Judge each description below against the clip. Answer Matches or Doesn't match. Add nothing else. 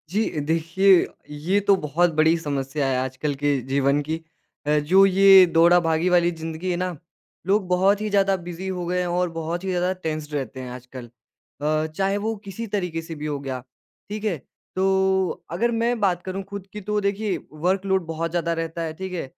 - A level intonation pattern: Doesn't match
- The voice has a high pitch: Doesn't match